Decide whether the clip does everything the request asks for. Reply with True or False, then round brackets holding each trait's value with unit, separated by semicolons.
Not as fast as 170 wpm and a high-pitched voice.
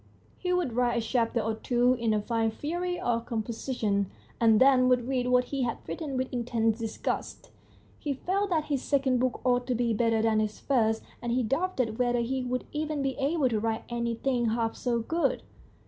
False (195 wpm; 245 Hz)